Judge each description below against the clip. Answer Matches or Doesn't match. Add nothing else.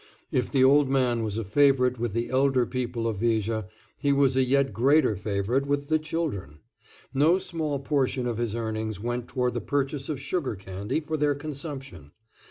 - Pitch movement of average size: Matches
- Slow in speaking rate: Doesn't match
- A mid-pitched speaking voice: Doesn't match